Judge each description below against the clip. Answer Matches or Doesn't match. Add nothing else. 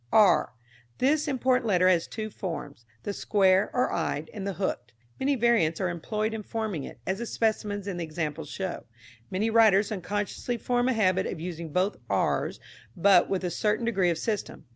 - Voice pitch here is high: Matches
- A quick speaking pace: Doesn't match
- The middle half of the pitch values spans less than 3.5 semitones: Doesn't match